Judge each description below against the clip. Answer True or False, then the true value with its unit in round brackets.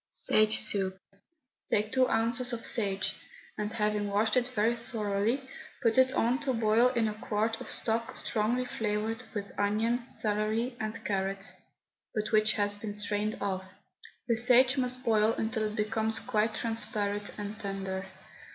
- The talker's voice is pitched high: True (220 Hz)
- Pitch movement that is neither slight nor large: False (2.0 semitones)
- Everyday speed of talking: True (150 wpm)